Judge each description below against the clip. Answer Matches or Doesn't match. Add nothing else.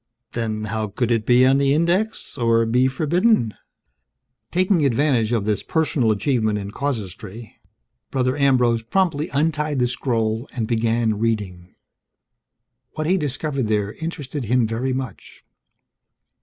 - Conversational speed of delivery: Doesn't match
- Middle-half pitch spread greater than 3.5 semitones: Matches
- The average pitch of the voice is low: Matches